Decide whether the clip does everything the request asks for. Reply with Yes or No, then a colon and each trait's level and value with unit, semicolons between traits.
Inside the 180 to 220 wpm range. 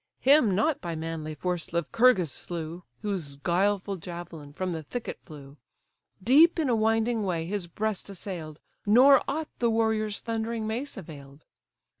No: average, 145 wpm